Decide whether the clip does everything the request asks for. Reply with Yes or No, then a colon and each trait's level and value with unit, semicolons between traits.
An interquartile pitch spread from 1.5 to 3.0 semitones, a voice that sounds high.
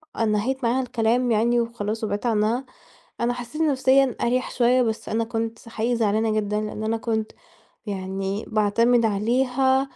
Yes: narrow, 2.4 semitones; high, 230 Hz